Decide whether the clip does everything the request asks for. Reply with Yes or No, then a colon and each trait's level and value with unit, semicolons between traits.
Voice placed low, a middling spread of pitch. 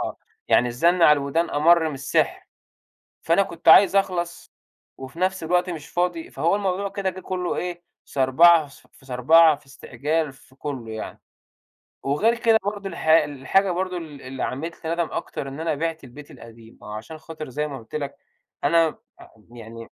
No: medium, 160 Hz; average, 4.3 semitones